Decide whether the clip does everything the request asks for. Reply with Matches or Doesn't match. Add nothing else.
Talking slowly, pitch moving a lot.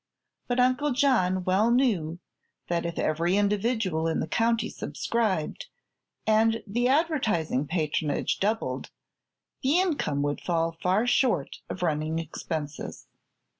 Matches